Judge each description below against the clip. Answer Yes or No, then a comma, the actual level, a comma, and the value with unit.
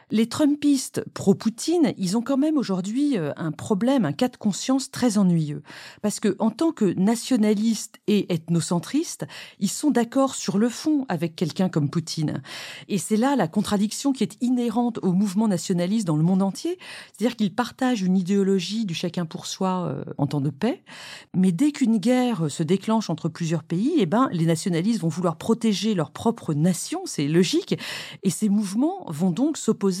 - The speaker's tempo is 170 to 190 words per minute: Yes, average, 180 wpm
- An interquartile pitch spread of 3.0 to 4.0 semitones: No, wide, 5.6 semitones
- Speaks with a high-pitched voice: Yes, high, 210 Hz